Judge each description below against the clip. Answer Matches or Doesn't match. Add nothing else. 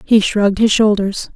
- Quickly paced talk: Doesn't match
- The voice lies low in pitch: Doesn't match